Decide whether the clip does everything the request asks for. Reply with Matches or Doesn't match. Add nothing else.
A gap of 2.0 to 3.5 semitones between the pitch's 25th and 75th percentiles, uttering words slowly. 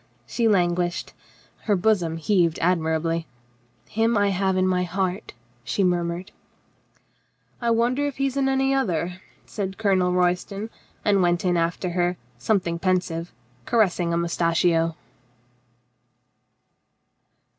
Matches